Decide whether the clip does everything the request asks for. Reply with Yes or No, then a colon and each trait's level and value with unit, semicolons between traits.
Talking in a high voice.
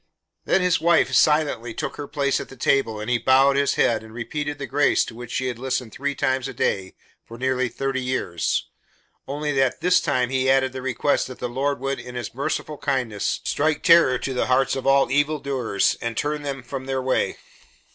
No: low, 130 Hz